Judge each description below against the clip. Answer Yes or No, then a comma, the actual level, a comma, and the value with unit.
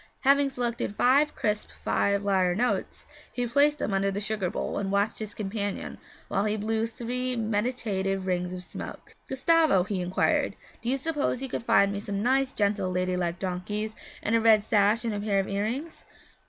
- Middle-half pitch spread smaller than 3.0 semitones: No, average, 3.9 semitones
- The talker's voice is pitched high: Yes, high, 210 Hz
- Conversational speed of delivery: Yes, average, 185 wpm